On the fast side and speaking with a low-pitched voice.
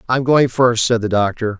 Yes: fast, 225 wpm; low, 115 Hz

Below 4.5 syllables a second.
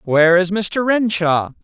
Yes: 4.1 syllables/s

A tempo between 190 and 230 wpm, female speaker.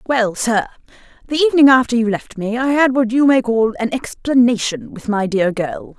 Yes: average, 200 wpm; female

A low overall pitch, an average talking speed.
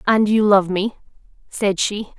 No: high, 205 Hz; average, 165 wpm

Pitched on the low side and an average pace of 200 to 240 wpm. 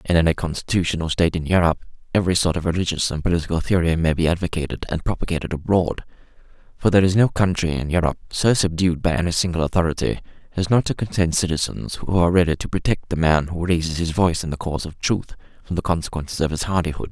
Yes: very low, 85 Hz; fast, 205 wpm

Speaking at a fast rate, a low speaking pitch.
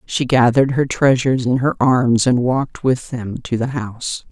No: average, 195 wpm; low, 125 Hz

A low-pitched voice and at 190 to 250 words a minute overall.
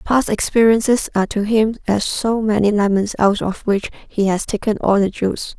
No: high, 210 Hz; average, 195 wpm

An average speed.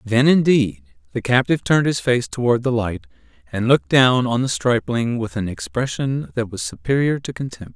Yes: average, 185 wpm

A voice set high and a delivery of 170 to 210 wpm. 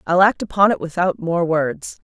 No: medium, 175 Hz; average, 200 wpm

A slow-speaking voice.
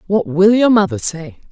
No: average, 200 wpm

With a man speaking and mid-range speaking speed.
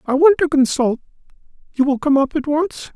Yes: male; average, 185 wpm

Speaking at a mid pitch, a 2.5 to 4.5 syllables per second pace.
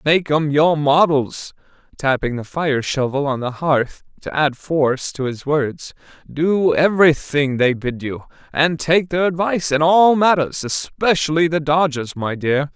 Yes: medium, 150 Hz; 4.2 syllables/s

